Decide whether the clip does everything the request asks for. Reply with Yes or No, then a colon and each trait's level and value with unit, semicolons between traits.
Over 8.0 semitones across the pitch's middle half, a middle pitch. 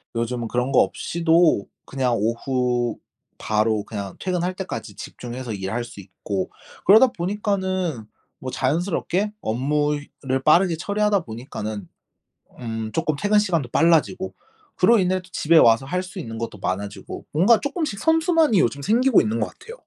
Yes: wide, 8.4 semitones; medium, 150 Hz